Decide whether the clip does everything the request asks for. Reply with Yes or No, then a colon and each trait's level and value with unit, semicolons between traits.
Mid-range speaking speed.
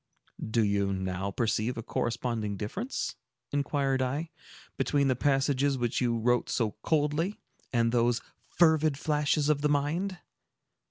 No: slow, 130 wpm